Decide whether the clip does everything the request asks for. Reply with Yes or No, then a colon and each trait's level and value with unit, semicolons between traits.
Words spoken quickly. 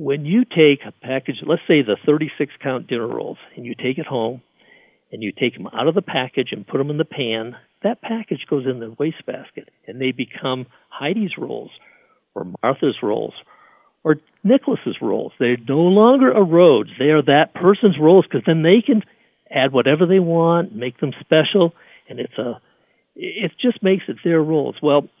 No: average, 190 wpm